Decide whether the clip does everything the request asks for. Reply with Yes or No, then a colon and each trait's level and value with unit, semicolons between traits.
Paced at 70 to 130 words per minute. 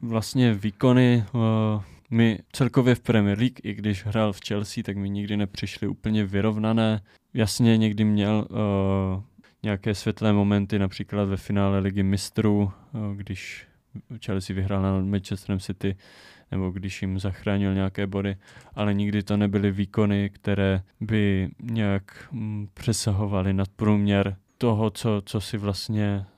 No: average, 140 wpm